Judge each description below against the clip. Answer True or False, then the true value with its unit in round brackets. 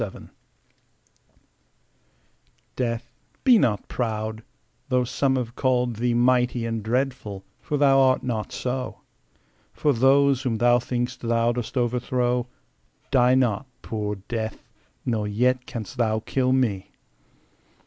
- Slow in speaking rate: True (120 wpm)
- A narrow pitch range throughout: True (2.3 semitones)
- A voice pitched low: True (120 Hz)